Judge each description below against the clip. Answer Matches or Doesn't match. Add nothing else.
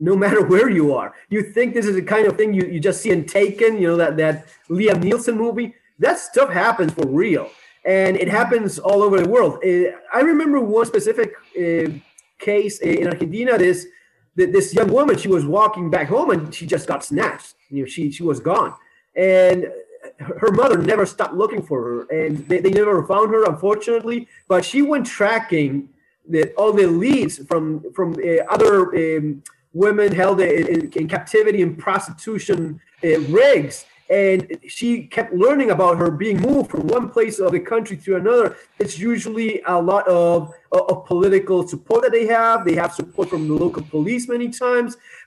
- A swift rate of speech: Doesn't match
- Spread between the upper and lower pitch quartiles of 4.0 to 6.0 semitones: Matches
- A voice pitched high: Matches